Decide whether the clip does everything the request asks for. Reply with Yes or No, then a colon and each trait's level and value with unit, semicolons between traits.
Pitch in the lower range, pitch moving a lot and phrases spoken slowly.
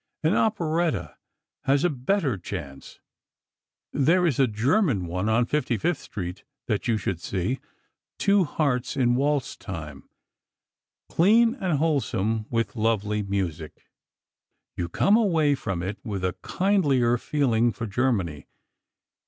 Yes: low, 120 Hz; wide, 7.7 semitones; slow, 120 wpm